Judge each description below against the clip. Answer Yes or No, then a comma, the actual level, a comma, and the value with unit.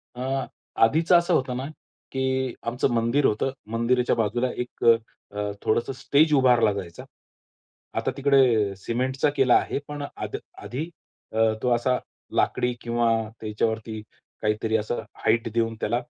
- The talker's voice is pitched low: Yes, low, 120 Hz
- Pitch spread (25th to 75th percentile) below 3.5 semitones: Yes, average, 2.8 semitones